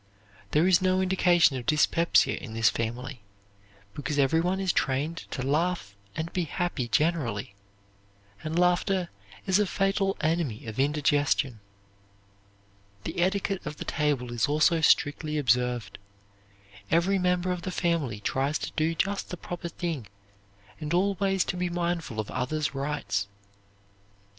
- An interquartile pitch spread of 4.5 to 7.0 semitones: Yes, average, 4.9 semitones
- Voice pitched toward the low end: No, medium, 155 Hz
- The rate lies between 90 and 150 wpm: Yes, average, 140 wpm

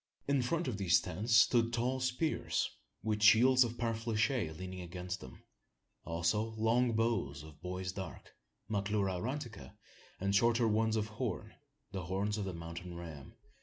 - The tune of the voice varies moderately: Yes, average, 4.4 semitones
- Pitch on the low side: Yes, low, 105 Hz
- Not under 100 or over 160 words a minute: Yes, average, 150 wpm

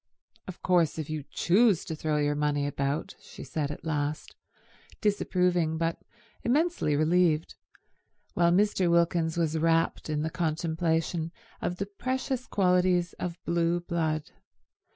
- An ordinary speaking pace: No, slow, 130 wpm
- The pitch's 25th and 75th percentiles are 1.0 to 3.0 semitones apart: Yes, narrow, 2.5 semitones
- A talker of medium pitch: Yes, medium, 165 Hz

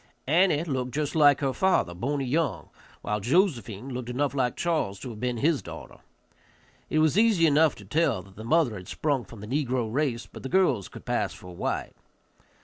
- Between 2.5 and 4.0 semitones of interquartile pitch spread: No, wide, 5.5 semitones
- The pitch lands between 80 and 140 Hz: Yes, low, 135 Hz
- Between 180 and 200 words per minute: Yes, average, 195 wpm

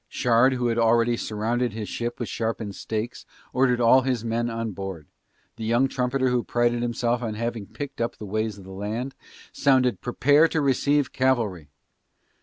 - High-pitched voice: No, low, 120 Hz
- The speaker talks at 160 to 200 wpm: Yes, average, 175 wpm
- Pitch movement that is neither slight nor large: No, narrow, 2.2 semitones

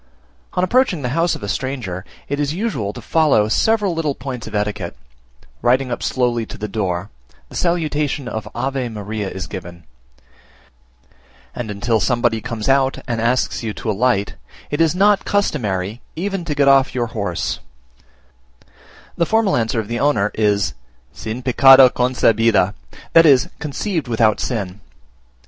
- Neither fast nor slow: Yes, average, 155 wpm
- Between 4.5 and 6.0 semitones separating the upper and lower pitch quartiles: Yes, wide, 5.6 semitones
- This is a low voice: Yes, low, 125 Hz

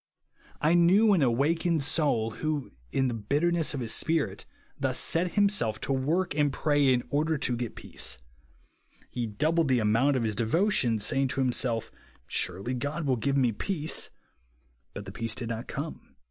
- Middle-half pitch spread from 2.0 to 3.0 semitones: No, average, 5.2 semitones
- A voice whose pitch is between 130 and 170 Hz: Yes, medium, 140 Hz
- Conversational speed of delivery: Yes, average, 170 wpm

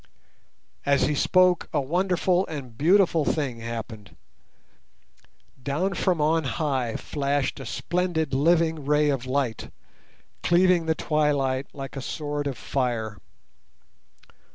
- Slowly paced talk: Yes, slow, 120 wpm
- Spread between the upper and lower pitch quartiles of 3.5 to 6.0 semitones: Yes, average, 3.9 semitones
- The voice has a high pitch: No, medium, 145 Hz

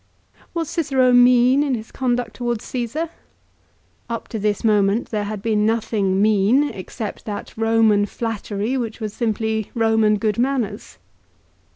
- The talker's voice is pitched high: Yes, high, 225 Hz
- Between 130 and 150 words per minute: Yes, average, 140 wpm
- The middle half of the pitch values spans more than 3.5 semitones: No, average, 2.7 semitones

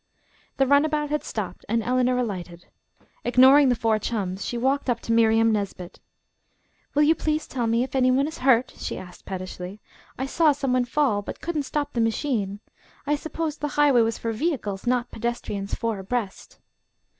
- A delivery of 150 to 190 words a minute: Yes, average, 180 wpm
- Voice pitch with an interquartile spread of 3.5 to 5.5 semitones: Yes, average, 4.8 semitones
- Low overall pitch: No, high, 245 Hz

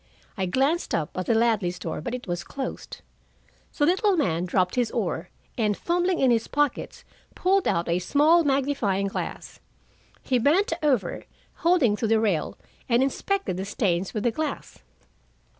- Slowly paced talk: No, average, 160 wpm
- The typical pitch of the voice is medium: No, high, 235 Hz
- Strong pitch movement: Yes, wide, 7.4 semitones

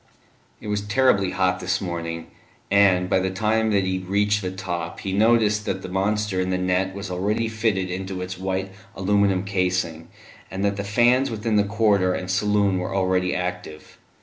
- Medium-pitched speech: No, very low, 95 Hz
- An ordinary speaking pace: Yes, average, 180 wpm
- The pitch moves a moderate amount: No, narrow, 2.1 semitones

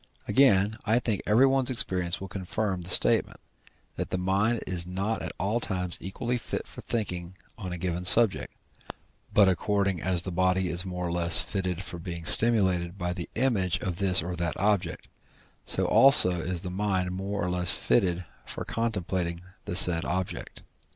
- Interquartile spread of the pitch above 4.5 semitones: No, narrow, 2.6 semitones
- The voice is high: No, very low, 95 Hz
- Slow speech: No, average, 170 wpm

